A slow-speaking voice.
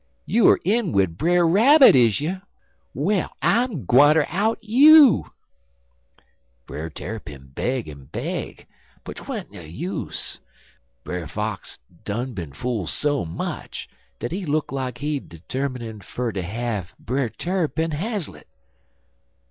Yes: slow, 125 wpm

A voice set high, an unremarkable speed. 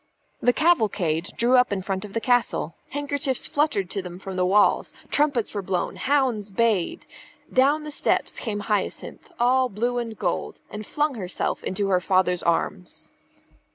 Yes: high, 215 Hz; average, 160 wpm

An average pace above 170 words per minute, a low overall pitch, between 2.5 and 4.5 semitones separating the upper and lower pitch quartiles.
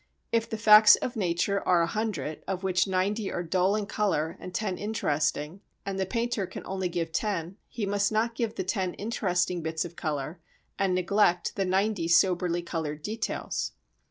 No: average, 180 wpm; high, 190 Hz; average, 3.6 semitones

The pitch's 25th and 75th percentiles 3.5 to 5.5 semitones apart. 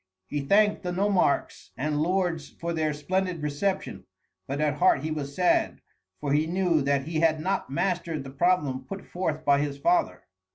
Yes: average, 4.0 semitones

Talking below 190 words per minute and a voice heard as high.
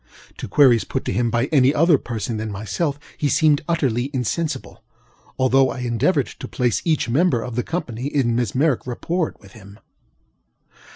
No: average, 160 wpm; low, 125 Hz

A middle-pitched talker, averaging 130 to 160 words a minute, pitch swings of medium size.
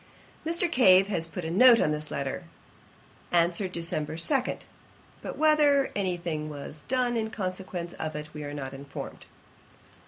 No: medium, 175 Hz; average, 155 wpm; wide, 7.1 semitones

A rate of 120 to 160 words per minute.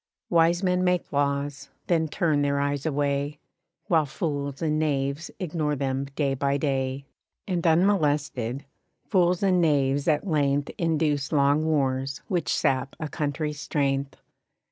Yes: slow, 135 wpm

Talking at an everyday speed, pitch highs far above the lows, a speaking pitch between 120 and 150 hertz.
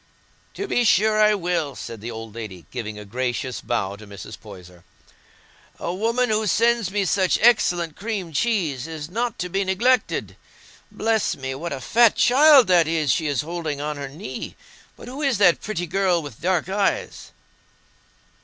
No: average, 170 wpm; wide, 7.9 semitones; medium, 175 Hz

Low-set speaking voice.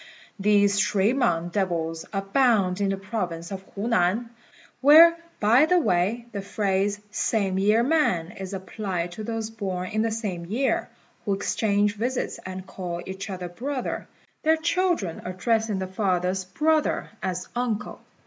No: high, 200 Hz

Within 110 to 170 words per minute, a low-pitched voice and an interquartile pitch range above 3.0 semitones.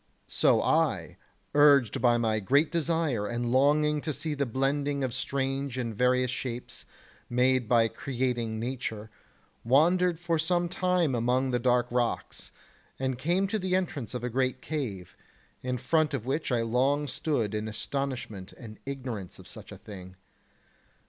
Yes: average, 155 wpm; low, 130 Hz; average, 3.7 semitones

